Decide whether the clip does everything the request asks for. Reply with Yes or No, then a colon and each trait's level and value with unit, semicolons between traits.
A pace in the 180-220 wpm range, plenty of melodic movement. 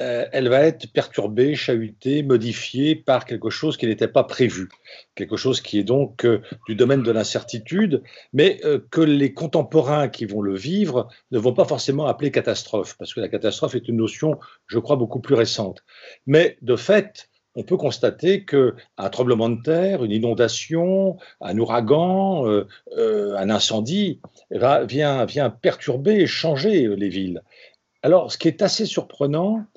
No: average, 155 wpm; wide, 7.3 semitones